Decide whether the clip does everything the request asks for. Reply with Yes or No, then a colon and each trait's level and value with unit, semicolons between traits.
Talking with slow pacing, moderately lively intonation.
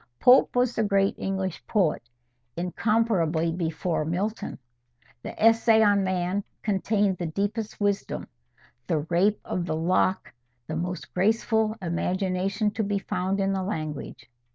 Yes: slow, 130 wpm; average, 3.2 semitones